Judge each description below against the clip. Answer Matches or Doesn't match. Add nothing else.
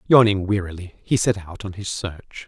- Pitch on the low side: Matches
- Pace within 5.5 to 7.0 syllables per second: Doesn't match